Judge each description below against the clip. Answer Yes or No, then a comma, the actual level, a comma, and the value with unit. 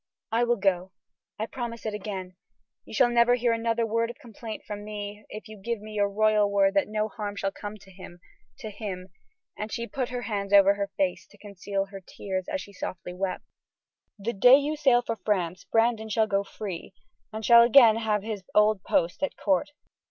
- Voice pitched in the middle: No, high, 210 Hz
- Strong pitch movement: No, average, 2.7 semitones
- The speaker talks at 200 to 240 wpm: Yes, fast, 205 wpm